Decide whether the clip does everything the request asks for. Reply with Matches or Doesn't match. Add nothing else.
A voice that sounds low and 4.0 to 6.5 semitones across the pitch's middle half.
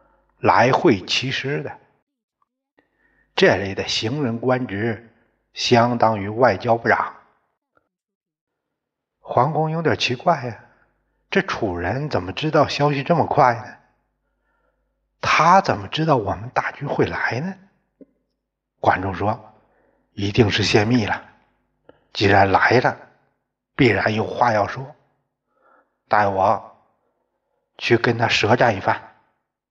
Matches